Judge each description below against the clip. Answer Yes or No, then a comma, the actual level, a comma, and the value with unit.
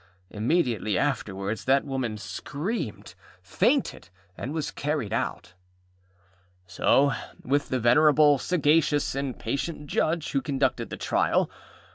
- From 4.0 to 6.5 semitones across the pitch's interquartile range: Yes, average, 4.4 semitones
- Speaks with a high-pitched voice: No, medium, 140 Hz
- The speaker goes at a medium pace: No, slow, 110 wpm